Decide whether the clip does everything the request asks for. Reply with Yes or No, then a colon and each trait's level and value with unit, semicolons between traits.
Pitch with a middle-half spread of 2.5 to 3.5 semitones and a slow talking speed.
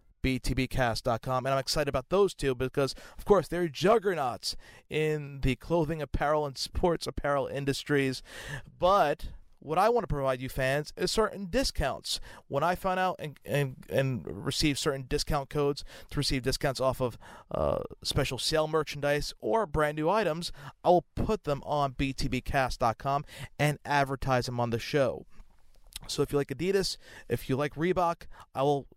No: average, 3.1 semitones; average, 160 wpm